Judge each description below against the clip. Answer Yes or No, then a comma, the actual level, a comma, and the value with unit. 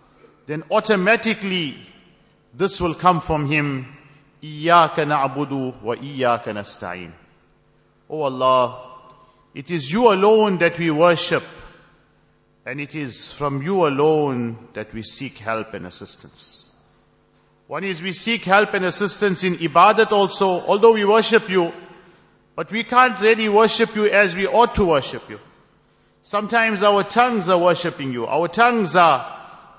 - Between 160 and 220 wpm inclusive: No, slow, 135 wpm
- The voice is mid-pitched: Yes, medium, 170 Hz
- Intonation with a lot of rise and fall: Yes, wide, 6.5 semitones